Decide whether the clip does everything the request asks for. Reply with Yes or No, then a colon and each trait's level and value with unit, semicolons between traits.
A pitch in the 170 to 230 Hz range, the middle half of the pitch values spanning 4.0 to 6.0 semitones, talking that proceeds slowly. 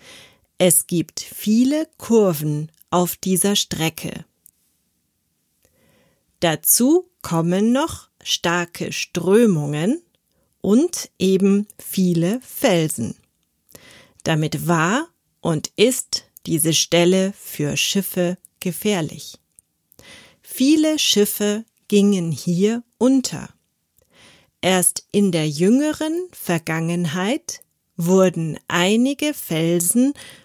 Yes: medium, 185 Hz; wide, 5.6 semitones; slow, 75 wpm